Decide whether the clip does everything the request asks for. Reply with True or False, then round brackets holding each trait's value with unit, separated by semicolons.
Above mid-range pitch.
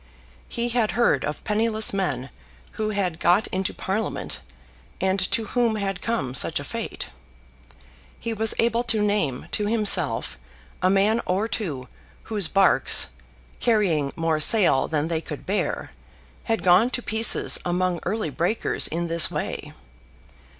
True (195 Hz)